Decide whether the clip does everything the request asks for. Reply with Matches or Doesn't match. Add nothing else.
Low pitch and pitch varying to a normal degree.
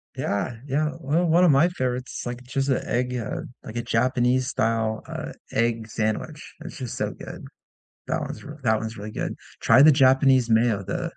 Matches